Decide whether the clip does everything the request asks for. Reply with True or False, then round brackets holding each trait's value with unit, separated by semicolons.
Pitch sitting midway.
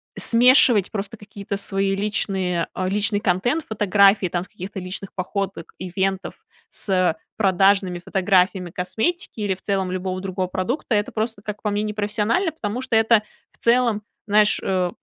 False (200 Hz)